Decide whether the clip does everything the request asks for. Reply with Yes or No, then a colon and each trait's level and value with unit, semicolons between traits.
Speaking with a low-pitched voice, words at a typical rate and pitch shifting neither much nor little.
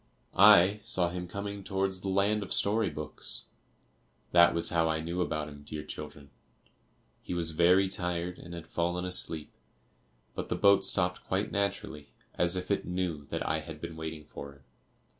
Yes: very low, 85 Hz; average, 175 wpm; average, 3.0 semitones